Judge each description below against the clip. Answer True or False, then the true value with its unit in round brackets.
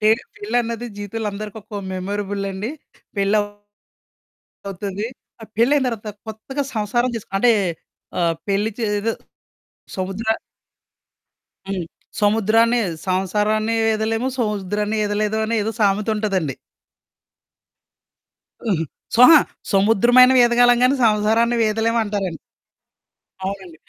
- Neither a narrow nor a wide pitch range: False (2.3 semitones)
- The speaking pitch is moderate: False (215 Hz)